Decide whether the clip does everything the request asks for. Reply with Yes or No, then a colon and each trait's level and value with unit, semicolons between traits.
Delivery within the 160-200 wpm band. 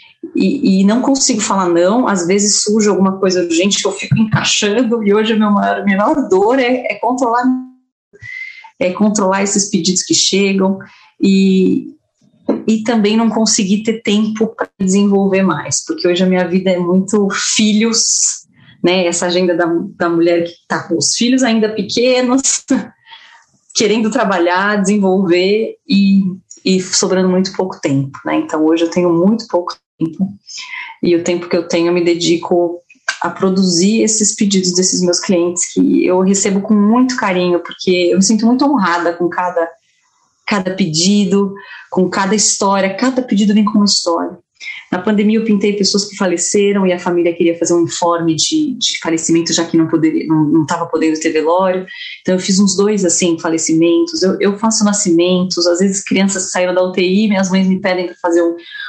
Yes: average, 175 wpm